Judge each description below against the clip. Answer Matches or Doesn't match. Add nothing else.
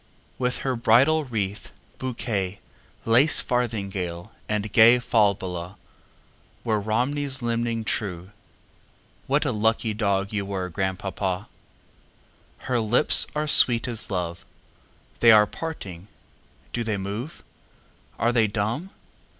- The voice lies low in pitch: Matches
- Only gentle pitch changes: Doesn't match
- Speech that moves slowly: Matches